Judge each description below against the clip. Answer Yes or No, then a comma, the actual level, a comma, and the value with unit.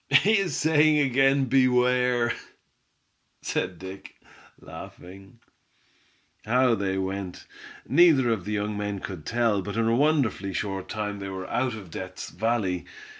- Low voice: Yes, low, 110 Hz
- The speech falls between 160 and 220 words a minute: No, slow, 135 wpm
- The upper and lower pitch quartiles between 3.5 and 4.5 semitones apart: No, average, 5.1 semitones